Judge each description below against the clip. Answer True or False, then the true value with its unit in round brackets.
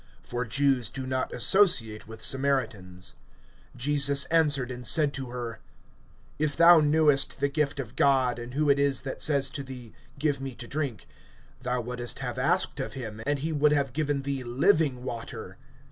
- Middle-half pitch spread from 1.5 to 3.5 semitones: True (2.9 semitones)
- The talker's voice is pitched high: False (135 Hz)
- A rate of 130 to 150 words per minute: False (175 wpm)